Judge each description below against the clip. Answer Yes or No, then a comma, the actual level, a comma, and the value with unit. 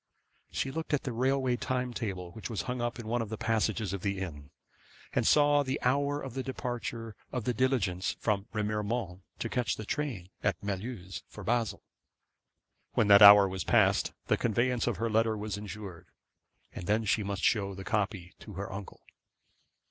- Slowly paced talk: No, average, 185 wpm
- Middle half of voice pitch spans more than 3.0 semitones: Yes, average, 3.9 semitones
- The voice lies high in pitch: No, low, 110 Hz